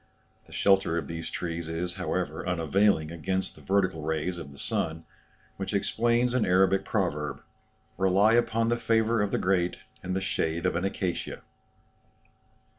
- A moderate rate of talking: Yes, average, 155 wpm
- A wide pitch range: No, average, 3.3 semitones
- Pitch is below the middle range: Yes, very low, 90 Hz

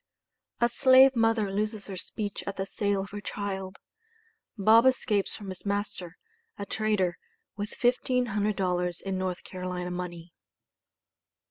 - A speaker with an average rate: No, slow, 130 wpm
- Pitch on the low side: No, high, 200 Hz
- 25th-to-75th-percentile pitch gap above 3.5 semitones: No, narrow, 2.6 semitones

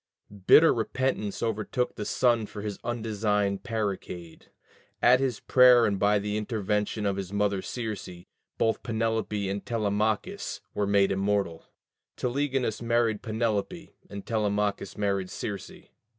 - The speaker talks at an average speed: No, slow, 125 wpm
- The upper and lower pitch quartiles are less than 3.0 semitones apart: Yes, narrow, 2.5 semitones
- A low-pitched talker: Yes, low, 105 Hz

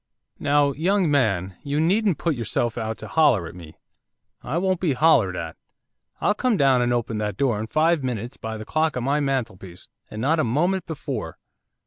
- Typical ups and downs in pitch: No, wide, 6.4 semitones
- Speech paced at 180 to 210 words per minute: Yes, average, 190 wpm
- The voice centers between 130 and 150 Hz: Yes, low, 135 Hz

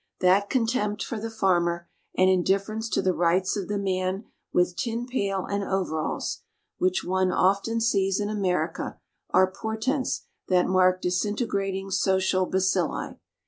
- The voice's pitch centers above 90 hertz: Yes, high, 190 Hz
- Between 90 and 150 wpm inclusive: Yes, average, 140 wpm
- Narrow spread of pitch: Yes, narrow, 2.2 semitones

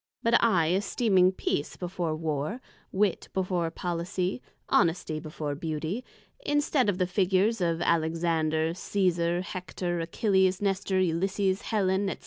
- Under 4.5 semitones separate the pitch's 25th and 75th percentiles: Yes, average, 2.8 semitones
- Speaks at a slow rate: Yes, slow, 120 wpm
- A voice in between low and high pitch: Yes, medium, 180 Hz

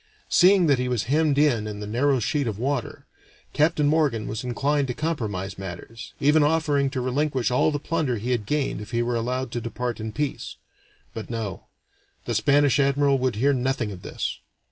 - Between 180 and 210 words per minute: Yes, average, 190 wpm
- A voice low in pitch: Yes, low, 130 Hz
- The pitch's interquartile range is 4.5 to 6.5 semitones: No, average, 4.1 semitones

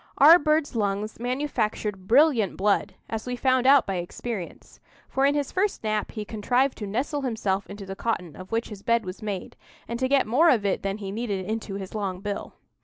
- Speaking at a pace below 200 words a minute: No, fast, 205 wpm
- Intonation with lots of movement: No, average, 4.6 semitones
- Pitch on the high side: Yes, high, 220 Hz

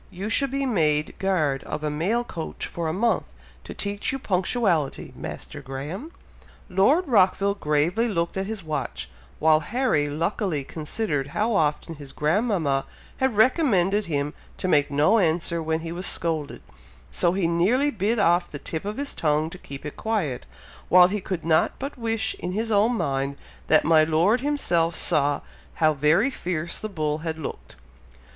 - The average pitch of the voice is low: No, medium, 175 Hz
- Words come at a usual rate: Yes, average, 170 wpm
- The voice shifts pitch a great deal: Yes, wide, 5.8 semitones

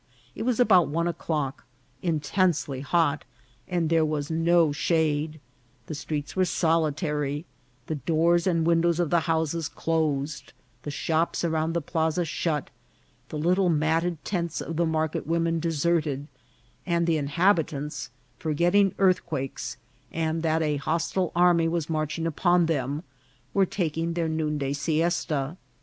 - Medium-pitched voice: Yes, medium, 160 Hz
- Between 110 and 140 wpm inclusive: Yes, slow, 135 wpm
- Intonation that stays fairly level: Yes, narrow, 2.1 semitones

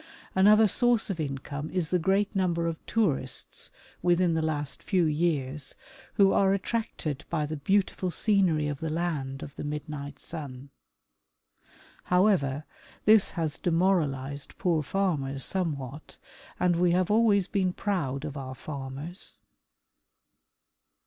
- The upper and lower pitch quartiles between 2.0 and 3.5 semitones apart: No, average, 4.9 semitones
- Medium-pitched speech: Yes, medium, 165 Hz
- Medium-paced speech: No, slow, 130 wpm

